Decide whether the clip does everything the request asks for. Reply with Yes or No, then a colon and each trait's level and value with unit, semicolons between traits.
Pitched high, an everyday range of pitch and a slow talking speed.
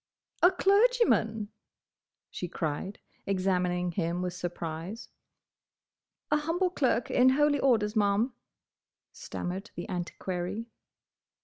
No: high, 205 Hz; wide, 6.9 semitones; slow, 95 wpm